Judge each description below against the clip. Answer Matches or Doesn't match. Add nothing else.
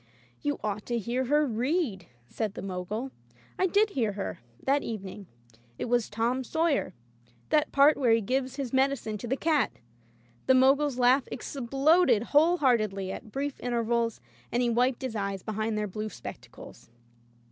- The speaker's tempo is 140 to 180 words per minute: Matches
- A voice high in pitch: Matches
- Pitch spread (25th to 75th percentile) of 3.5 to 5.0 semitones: Matches